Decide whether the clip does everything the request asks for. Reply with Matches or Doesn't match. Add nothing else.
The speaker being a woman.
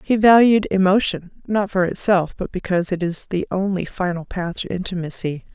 Matches